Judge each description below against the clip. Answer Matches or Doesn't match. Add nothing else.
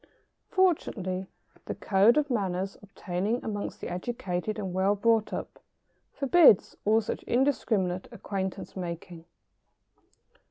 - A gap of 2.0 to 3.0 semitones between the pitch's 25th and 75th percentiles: Doesn't match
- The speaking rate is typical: Doesn't match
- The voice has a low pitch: Doesn't match